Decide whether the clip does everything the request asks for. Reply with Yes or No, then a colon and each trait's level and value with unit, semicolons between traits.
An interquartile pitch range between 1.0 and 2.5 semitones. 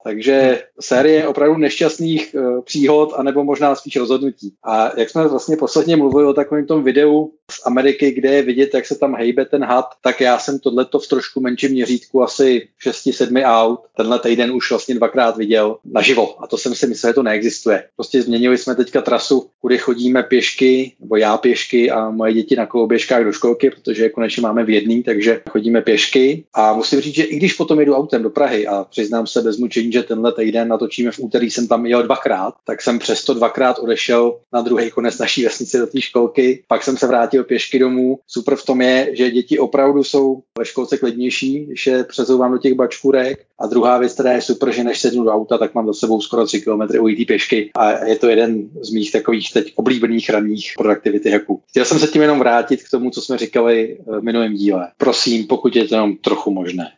No: average, 2.9 semitones